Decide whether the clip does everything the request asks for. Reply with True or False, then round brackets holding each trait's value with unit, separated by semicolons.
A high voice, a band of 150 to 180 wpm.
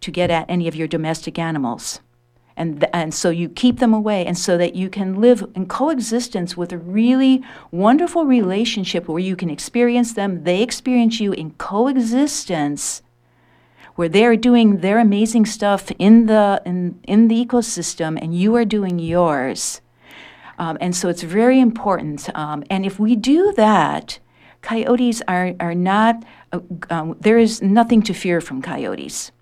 True (195 Hz; 165 wpm)